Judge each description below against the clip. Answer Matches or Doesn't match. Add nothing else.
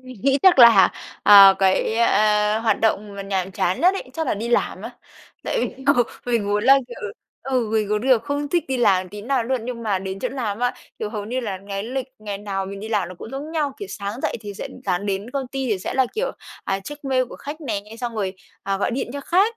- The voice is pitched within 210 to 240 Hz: Matches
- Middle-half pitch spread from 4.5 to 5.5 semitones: Matches